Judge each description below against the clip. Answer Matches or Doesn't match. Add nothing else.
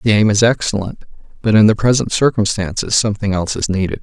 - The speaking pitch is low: Matches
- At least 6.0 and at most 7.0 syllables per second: Matches